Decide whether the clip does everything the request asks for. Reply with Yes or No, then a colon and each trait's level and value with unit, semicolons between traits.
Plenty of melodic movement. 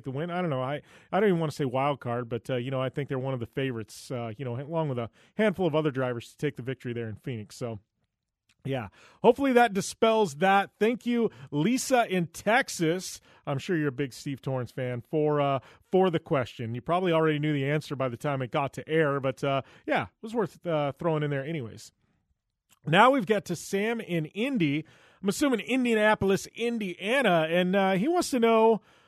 Yes: wide, 6.8 semitones